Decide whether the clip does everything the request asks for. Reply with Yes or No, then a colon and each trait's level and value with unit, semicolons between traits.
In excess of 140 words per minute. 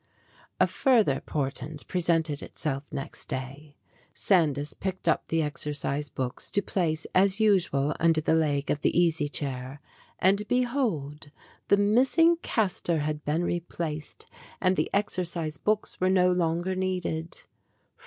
No: slow, 135 wpm